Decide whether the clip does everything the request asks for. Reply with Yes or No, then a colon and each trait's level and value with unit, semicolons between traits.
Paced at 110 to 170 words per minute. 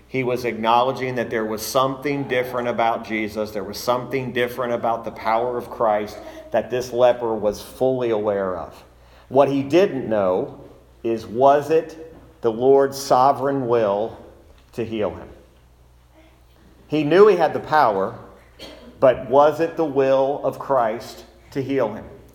Yes: average, 150 wpm